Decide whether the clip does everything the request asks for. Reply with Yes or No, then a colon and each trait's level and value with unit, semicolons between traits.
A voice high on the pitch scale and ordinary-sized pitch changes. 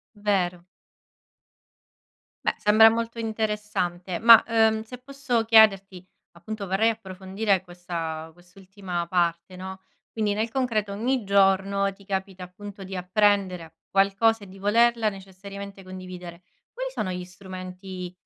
Yes: high, 195 Hz; average, 3.0 semitones